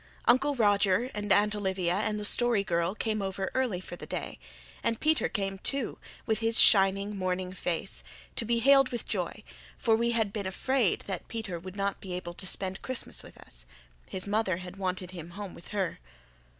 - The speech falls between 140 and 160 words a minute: No, average, 190 wpm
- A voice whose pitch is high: Yes, high, 200 Hz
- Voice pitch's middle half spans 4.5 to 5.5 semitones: No, average, 3.4 semitones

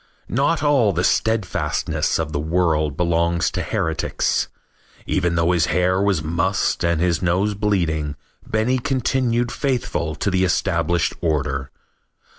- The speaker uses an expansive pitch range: No, average, 4.1 semitones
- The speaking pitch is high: No, very low, 90 Hz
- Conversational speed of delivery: No, slow, 130 wpm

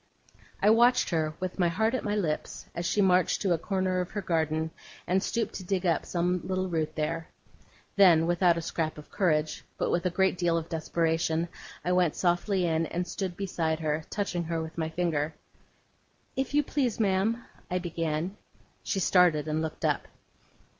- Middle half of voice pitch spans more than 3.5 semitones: No, average, 2.9 semitones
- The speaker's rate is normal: Yes, average, 185 wpm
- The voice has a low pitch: No, medium, 175 Hz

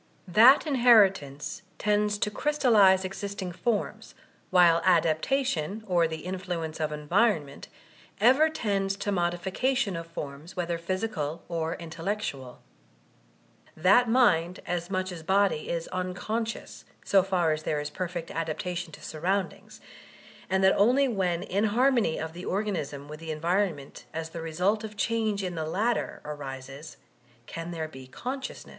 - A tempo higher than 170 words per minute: No, average, 140 wpm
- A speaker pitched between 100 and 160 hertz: No, medium, 180 Hz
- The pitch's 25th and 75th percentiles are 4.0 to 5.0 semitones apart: Yes, average, 4.4 semitones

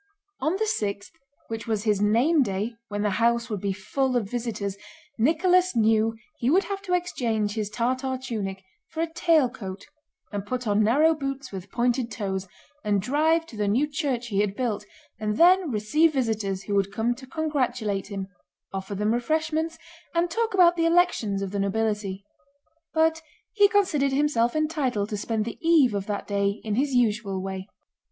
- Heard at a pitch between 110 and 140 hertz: No, high, 235 Hz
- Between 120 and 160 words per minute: No, average, 180 wpm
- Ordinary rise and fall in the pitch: No, wide, 6.9 semitones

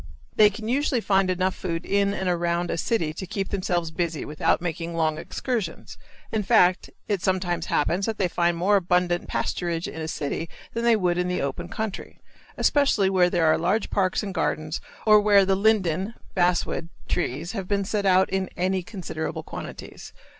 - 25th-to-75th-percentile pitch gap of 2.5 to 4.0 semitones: Yes, average, 2.8 semitones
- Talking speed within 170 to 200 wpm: Yes, average, 180 wpm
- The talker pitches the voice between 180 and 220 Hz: Yes, medium, 185 Hz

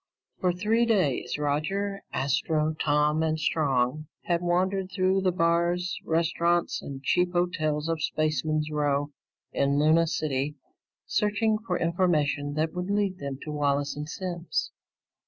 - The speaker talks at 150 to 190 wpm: No, slow, 135 wpm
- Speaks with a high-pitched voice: No, medium, 160 Hz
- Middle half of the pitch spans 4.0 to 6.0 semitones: No, average, 3.4 semitones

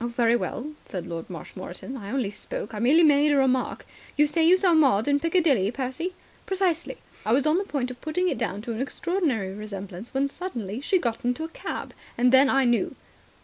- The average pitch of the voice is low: No, very high, 265 Hz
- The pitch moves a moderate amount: No, wide, 5.9 semitones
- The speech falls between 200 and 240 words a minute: Yes, fast, 205 wpm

